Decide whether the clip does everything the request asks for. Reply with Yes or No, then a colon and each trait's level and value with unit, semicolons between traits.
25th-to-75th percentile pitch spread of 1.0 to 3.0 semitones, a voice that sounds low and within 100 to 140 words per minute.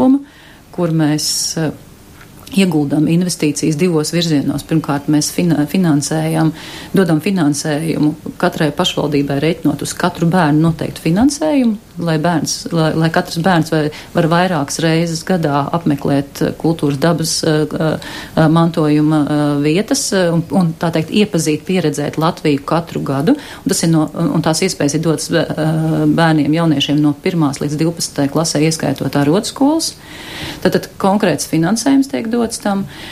No: average, 2.7 semitones; medium, 160 Hz; average, 130 wpm